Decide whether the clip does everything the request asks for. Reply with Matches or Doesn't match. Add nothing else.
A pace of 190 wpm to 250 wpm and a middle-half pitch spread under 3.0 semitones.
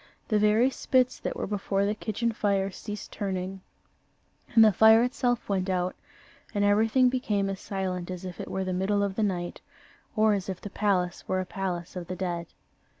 Matches